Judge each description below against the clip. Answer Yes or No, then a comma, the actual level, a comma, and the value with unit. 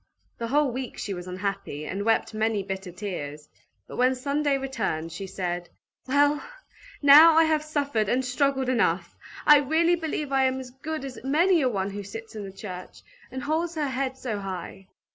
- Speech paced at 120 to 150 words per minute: No, average, 185 wpm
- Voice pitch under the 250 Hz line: No, very high, 255 Hz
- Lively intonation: Yes, wide, 6.6 semitones